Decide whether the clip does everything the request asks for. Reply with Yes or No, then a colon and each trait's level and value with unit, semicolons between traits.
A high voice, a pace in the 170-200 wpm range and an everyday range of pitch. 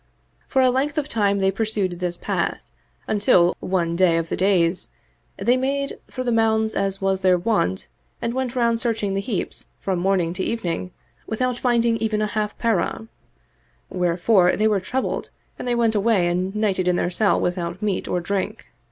Yes: high, 200 Hz; average, 180 wpm; average, 4.2 semitones